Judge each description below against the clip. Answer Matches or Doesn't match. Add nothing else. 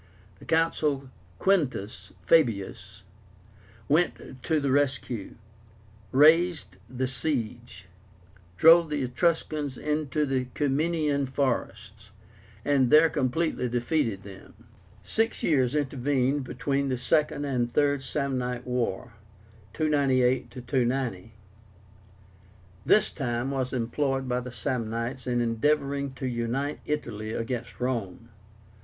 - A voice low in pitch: Matches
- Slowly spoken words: Matches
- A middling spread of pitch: Matches